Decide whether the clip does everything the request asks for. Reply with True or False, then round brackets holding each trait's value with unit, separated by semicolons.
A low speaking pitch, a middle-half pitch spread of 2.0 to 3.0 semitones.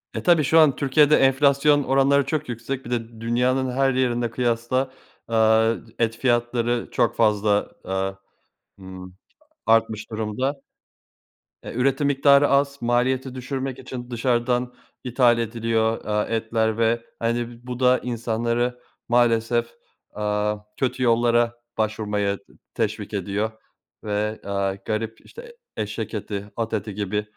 True (120 Hz; 2.7 semitones)